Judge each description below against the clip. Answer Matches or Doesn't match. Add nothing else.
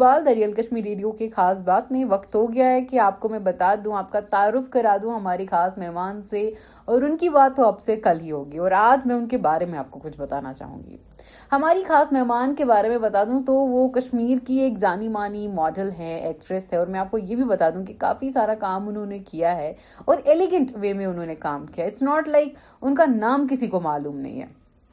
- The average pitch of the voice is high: Matches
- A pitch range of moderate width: Doesn't match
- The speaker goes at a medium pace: Doesn't match